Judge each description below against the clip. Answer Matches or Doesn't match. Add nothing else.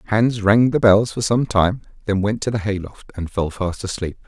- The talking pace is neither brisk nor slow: Doesn't match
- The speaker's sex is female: Doesn't match